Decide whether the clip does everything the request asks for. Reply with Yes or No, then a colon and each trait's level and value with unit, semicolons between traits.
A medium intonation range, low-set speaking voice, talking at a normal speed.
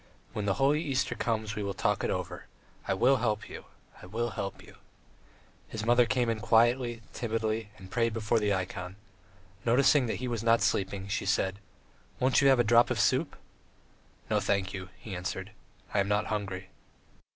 Yes: average, 3.4 semitones; low, 110 Hz; average, 185 wpm